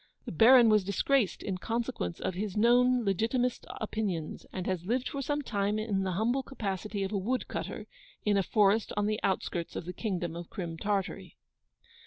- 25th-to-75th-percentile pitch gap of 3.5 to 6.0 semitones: Yes, average, 3.8 semitones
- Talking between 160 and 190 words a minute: Yes, average, 185 wpm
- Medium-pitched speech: No, high, 210 Hz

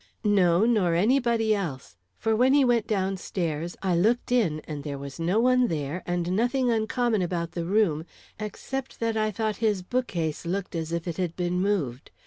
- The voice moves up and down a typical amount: Yes, average, 5.0 semitones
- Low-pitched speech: No, high, 190 Hz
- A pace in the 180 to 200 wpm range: Yes, average, 185 wpm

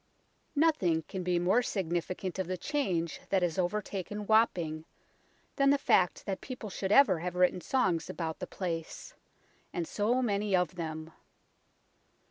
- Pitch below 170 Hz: No, medium, 185 Hz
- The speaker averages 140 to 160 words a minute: Yes, average, 150 wpm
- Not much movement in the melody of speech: No, average, 3.5 semitones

